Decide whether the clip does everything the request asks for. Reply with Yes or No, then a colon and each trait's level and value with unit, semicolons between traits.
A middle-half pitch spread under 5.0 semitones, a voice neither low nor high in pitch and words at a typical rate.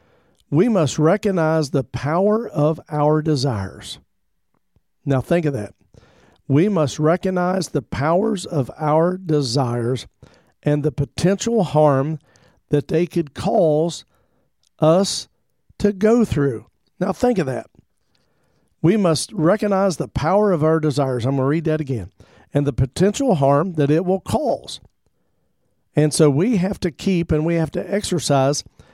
Yes: average, 4.4 semitones; medium, 155 Hz; average, 145 wpm